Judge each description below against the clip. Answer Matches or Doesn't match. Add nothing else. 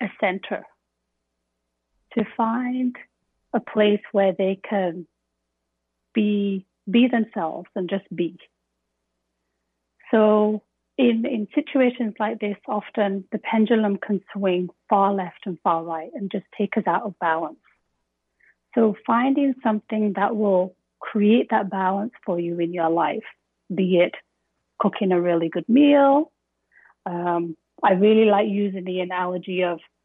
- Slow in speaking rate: Matches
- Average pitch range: Matches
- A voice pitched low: Doesn't match